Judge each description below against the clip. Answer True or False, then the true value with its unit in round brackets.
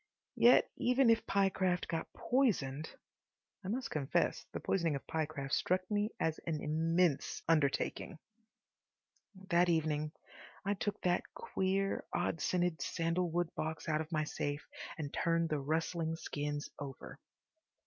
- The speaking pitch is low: False (165 Hz)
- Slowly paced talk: True (130 wpm)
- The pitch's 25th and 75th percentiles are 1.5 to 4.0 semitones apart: True (3.4 semitones)